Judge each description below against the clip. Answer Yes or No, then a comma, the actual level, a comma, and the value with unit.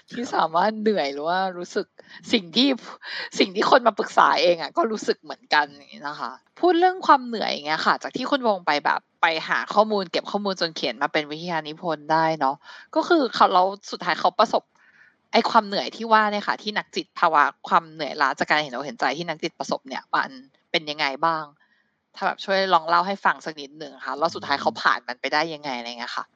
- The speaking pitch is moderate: Yes, medium, 180 Hz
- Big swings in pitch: Yes, wide, 6.2 semitones